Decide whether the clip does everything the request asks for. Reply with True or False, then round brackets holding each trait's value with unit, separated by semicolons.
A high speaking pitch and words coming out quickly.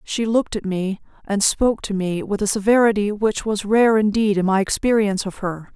True (205 Hz; 210 wpm)